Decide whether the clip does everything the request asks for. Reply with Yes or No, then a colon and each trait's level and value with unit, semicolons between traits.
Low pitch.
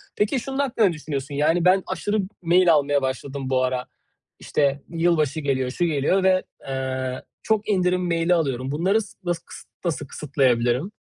No: medium, 155 Hz